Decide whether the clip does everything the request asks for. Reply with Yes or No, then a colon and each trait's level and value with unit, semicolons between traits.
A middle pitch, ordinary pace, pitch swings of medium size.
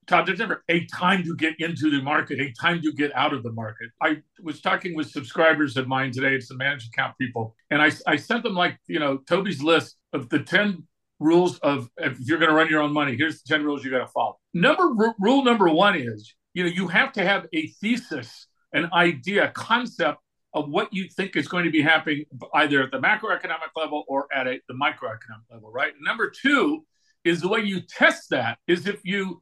No: medium, 160 Hz; fast, 225 wpm; average, 5.0 semitones